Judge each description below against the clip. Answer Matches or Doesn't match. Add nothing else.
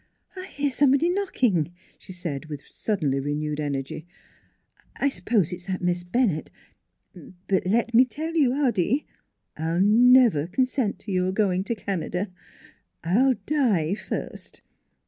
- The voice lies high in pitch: Matches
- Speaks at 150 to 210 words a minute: Doesn't match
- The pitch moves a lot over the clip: Matches